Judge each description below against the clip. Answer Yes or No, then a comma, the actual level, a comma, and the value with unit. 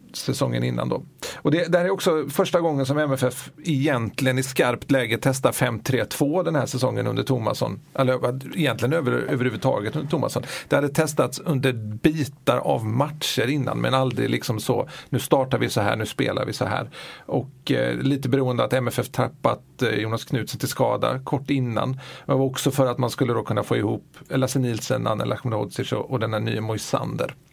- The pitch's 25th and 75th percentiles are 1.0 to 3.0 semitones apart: Yes, average, 2.7 semitones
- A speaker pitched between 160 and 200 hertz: No, low, 130 Hz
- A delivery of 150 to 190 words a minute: Yes, average, 185 wpm